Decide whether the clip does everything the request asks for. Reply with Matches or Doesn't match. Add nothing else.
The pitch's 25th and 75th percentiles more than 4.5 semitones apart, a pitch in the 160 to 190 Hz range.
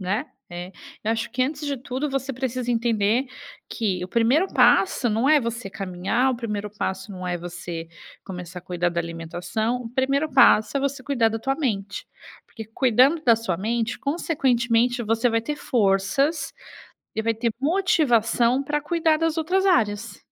Doesn't match